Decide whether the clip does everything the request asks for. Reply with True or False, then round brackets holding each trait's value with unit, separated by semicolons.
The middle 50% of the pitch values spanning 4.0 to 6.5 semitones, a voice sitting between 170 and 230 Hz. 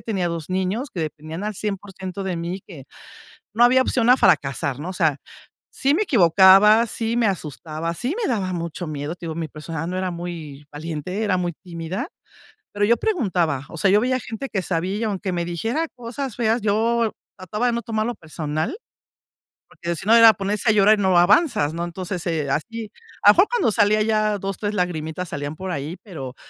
True (4.7 semitones; 190 Hz)